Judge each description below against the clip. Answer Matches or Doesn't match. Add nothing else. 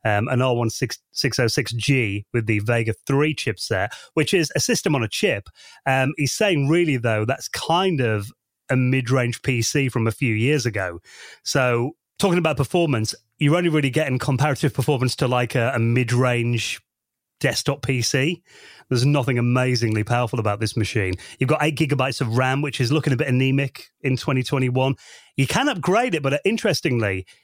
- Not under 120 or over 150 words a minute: Doesn't match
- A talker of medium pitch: Doesn't match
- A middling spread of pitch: Matches